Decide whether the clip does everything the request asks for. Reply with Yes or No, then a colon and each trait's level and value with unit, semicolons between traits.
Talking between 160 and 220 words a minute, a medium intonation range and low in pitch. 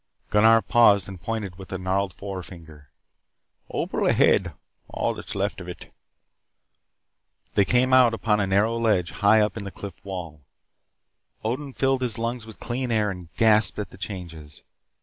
Yes: average, 165 wpm; average, 3.5 semitones; low, 105 Hz